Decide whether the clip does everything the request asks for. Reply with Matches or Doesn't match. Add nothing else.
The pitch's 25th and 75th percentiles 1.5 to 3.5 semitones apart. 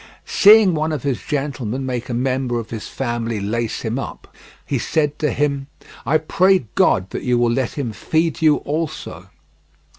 Doesn't match